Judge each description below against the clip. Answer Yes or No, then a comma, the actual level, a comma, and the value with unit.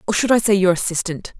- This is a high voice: Yes, high, 195 Hz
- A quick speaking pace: Yes, fast, 260 wpm